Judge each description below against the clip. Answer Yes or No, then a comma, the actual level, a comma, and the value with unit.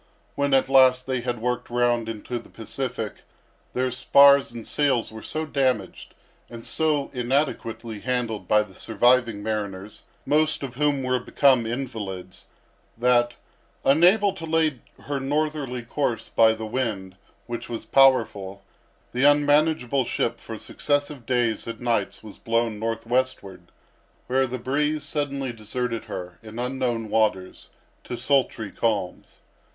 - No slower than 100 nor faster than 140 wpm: Yes, slow, 135 wpm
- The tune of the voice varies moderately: Yes, average, 3.5 semitones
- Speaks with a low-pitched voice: Yes, low, 125 Hz